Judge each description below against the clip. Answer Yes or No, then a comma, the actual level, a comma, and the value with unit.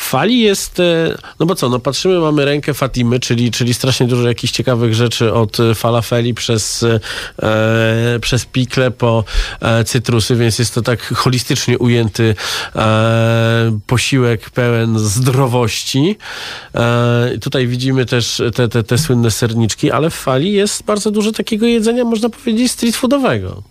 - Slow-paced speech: No, average, 145 wpm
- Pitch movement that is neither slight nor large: Yes, average, 3.3 semitones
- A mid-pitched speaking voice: No, low, 125 Hz